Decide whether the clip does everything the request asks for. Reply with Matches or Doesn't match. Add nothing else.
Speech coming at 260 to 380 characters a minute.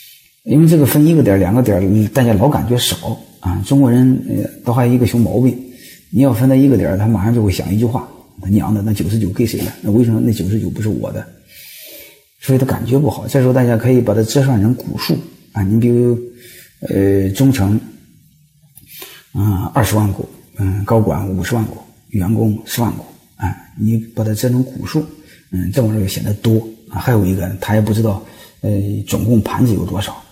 Matches